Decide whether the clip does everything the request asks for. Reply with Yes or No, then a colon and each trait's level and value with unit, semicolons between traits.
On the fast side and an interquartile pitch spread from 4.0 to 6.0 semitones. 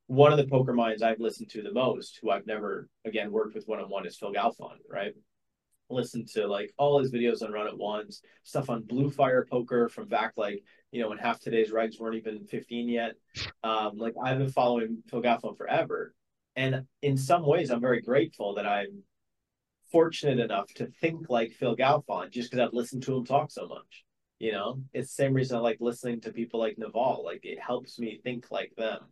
No: fast, 210 wpm; narrow, 2.6 semitones